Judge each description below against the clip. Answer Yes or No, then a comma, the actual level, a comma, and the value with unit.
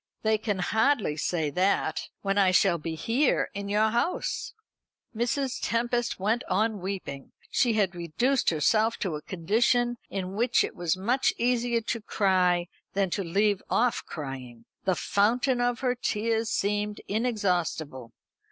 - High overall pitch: Yes, high, 205 Hz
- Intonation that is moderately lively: Yes, average, 4.6 semitones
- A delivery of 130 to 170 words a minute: Yes, average, 145 wpm